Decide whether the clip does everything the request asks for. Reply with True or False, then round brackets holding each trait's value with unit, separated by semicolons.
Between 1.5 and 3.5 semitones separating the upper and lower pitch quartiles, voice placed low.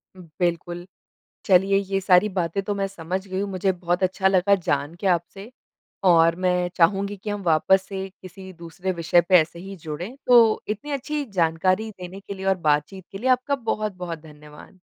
False (2.5 semitones; 185 Hz)